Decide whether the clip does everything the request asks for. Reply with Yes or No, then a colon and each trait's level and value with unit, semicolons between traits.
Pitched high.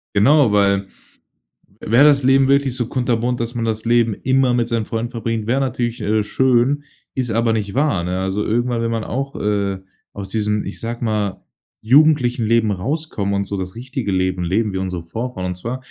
No: low, 115 Hz